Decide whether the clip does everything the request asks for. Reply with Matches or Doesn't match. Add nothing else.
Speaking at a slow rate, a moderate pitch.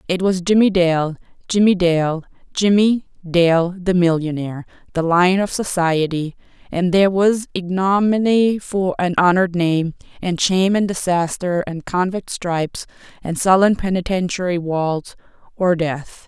Matches